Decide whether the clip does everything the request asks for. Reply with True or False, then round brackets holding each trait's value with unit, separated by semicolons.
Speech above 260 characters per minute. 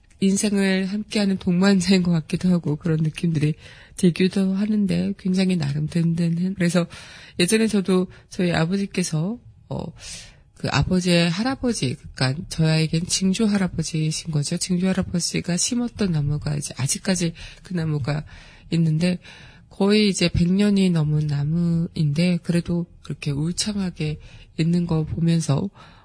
True (310 characters per minute)